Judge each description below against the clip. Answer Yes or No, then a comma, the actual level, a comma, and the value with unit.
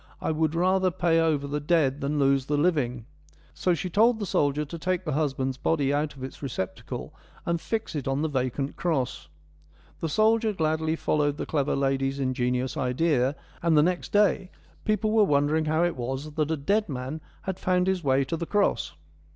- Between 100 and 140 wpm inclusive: No, average, 195 wpm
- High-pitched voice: No, medium, 150 Hz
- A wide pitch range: No, average, 4.2 semitones